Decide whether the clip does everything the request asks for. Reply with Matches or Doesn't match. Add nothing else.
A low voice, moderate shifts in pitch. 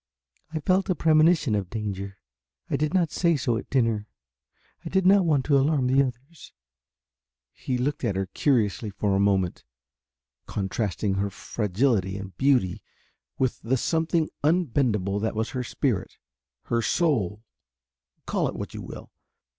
Doesn't match